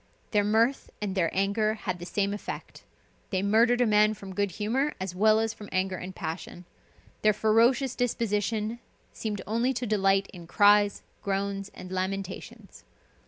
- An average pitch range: No, narrow, 2.3 semitones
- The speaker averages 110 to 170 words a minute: Yes, average, 160 wpm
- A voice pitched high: Yes, high, 205 Hz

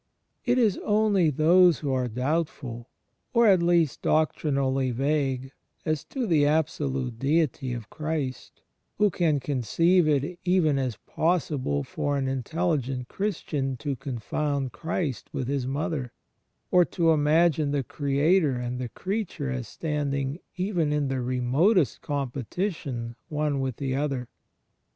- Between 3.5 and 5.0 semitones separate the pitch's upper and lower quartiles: Yes, average, 4.1 semitones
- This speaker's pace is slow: Yes, slow, 130 wpm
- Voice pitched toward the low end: No, medium, 145 Hz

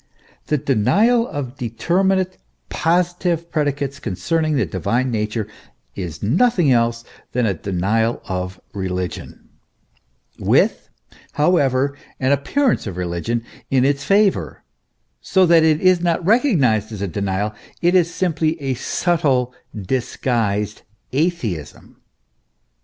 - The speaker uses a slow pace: Yes, slow, 115 wpm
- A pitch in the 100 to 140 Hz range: Yes, low, 135 Hz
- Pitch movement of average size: No, wide, 8.0 semitones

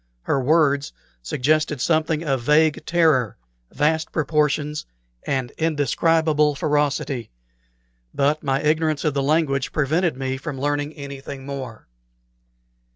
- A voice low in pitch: No, medium, 145 Hz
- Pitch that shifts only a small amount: Yes, narrow, 2.2 semitones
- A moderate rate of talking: No, slow, 110 wpm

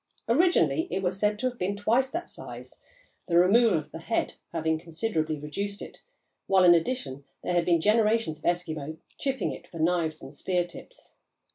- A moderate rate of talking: Yes, average, 180 wpm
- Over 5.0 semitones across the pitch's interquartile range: Yes, wide, 5.6 semitones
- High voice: No, medium, 180 Hz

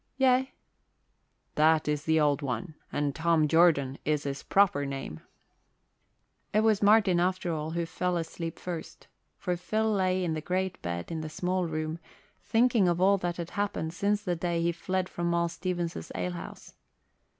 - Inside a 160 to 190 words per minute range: Yes, average, 165 wpm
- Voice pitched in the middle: Yes, medium, 170 Hz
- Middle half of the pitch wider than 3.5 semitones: No, average, 3.1 semitones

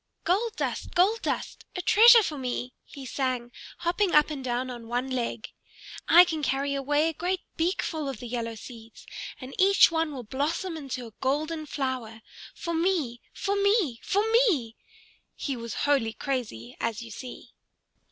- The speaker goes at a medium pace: Yes, average, 165 wpm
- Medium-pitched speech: No, very high, 275 Hz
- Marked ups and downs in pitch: Yes, wide, 5.8 semitones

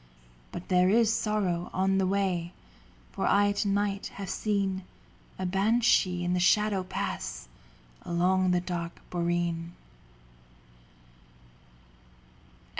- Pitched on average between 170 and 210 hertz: Yes, medium, 185 Hz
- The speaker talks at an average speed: No, slow, 110 wpm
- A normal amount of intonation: No, narrow, 2.3 semitones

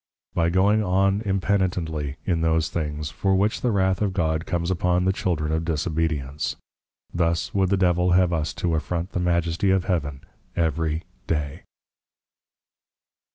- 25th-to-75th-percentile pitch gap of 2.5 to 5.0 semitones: Yes, average, 2.9 semitones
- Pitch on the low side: Yes, very low, 85 Hz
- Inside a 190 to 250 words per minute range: No, average, 150 wpm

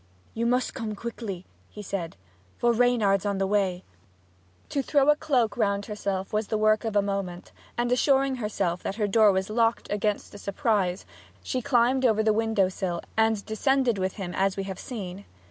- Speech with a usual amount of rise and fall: Yes, average, 3.3 semitones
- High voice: Yes, high, 210 Hz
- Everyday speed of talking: Yes, average, 185 wpm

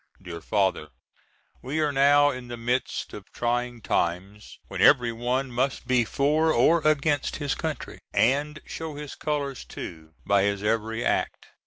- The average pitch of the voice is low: Yes, low, 125 Hz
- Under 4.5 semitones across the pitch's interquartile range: No, average, 4.8 semitones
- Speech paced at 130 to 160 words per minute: Yes, average, 155 wpm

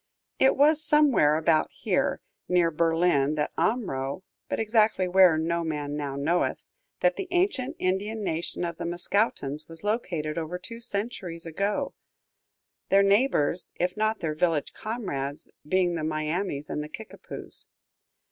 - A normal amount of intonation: No, wide, 5.7 semitones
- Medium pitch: Yes, medium, 175 Hz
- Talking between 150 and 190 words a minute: No, average, 140 wpm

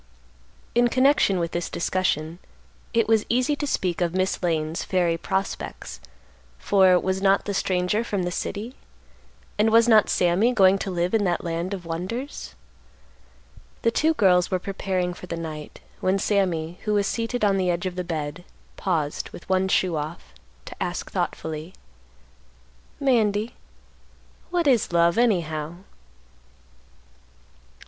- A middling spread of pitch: Yes, average, 3.7 semitones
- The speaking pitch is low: No, medium, 185 Hz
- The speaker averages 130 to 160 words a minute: Yes, average, 145 wpm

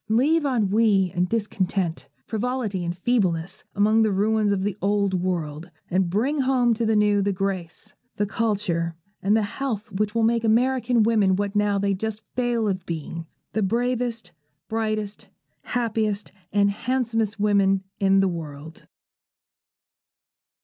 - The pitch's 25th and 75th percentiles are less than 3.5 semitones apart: Yes, average, 3.0 semitones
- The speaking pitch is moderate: No, high, 205 Hz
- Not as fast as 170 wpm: Yes, average, 140 wpm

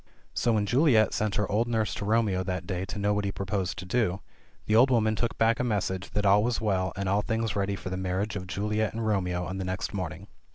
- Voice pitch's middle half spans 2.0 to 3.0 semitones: Yes, average, 2.7 semitones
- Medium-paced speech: No, fast, 250 wpm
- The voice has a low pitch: Yes, low, 100 Hz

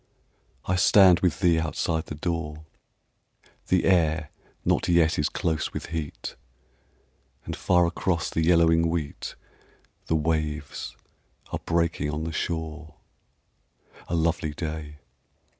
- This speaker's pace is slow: Yes, slow, 120 wpm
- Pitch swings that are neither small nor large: No, narrow, 1.7 semitones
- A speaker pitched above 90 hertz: No, very low, 80 Hz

